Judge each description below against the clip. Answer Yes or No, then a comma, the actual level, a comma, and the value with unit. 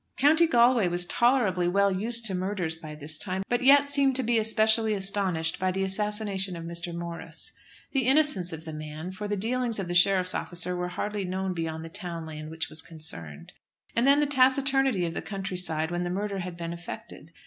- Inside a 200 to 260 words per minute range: Yes, fast, 205 wpm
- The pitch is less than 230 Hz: Yes, high, 190 Hz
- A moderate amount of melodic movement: Yes, average, 4.9 semitones